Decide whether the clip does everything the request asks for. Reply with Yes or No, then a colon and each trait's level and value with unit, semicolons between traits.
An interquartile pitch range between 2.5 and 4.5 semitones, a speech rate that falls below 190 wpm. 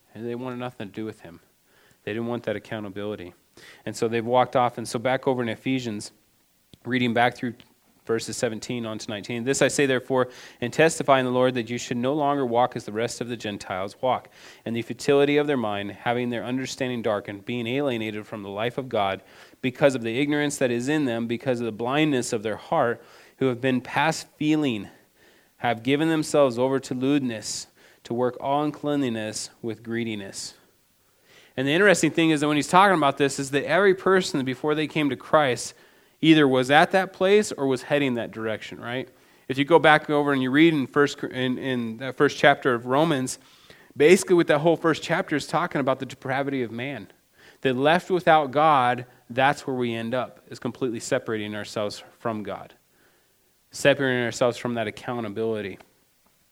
No: average, 3.7 semitones; average, 195 wpm